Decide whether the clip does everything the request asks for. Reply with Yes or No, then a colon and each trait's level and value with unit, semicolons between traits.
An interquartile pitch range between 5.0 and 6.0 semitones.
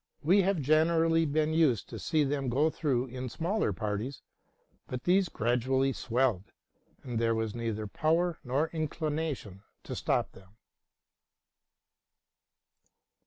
Yes: average, 5.3 semitones